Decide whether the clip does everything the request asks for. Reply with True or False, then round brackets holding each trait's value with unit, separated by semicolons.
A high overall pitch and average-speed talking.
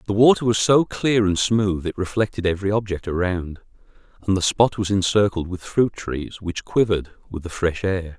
False (100 Hz; 190 wpm)